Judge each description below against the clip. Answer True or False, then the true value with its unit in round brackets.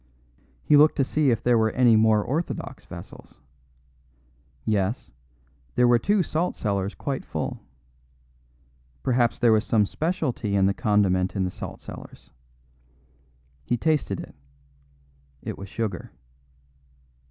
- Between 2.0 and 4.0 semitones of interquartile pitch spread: False (5.1 semitones)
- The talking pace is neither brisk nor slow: False (130 wpm)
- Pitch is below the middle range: True (115 Hz)